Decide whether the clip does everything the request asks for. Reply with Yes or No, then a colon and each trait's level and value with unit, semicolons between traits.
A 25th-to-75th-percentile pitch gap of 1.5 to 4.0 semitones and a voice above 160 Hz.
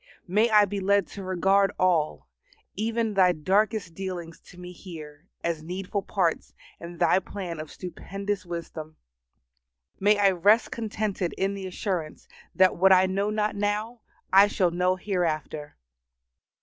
Yes: average, 2.8 semitones; high, 190 Hz